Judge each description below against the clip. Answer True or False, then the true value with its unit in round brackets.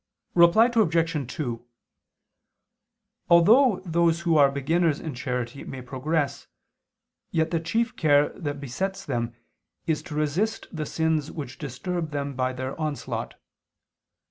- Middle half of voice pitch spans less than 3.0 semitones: False (3.7 semitones)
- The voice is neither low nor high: True (155 Hz)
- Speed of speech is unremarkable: False (125 wpm)